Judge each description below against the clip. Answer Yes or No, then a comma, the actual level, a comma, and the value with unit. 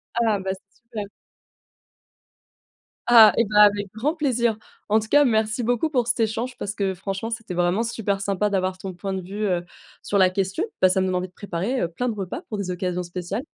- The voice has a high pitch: Yes, high, 205 Hz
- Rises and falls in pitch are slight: No, average, 3.4 semitones